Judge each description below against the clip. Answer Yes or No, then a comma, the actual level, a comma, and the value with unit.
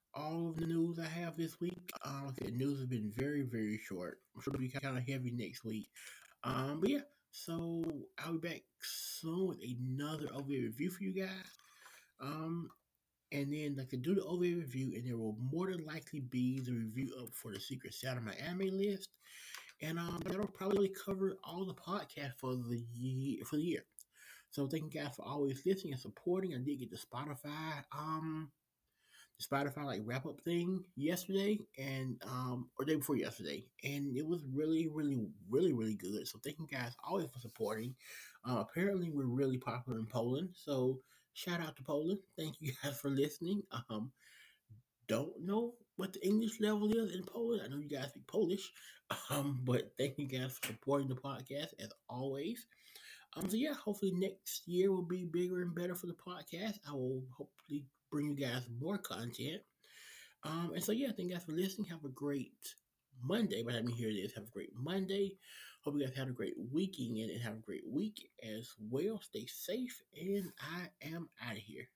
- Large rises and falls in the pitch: Yes, wide, 5.7 semitones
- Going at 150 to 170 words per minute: No, average, 195 wpm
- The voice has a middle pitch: Yes, medium, 145 Hz